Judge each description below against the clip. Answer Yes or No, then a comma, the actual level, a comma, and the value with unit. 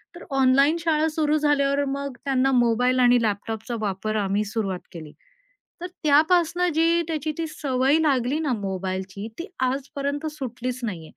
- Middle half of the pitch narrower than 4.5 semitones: No, wide, 5.5 semitones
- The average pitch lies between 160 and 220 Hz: No, very high, 265 Hz